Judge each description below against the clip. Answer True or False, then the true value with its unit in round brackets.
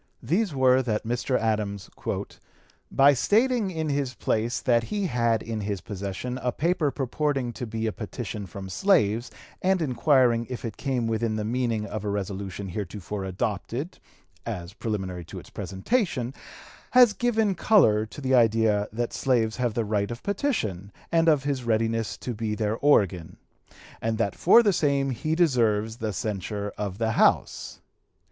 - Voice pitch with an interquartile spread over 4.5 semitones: True (4.9 semitones)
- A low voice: True (115 Hz)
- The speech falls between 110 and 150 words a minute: False (160 wpm)